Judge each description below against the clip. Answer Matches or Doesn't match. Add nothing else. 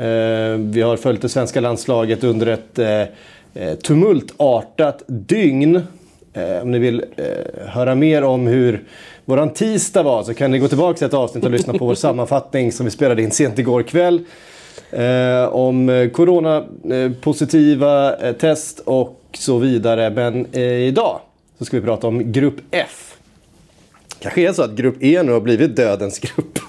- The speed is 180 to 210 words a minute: Doesn't match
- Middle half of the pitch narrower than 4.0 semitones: Matches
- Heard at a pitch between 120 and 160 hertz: Matches